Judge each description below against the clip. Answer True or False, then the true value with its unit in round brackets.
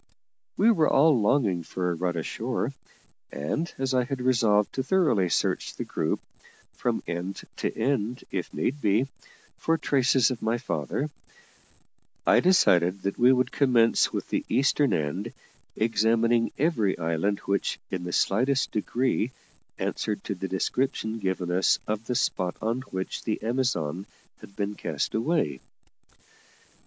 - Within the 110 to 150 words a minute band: True (145 wpm)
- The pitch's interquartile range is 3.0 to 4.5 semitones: False (5.6 semitones)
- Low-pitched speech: True (110 Hz)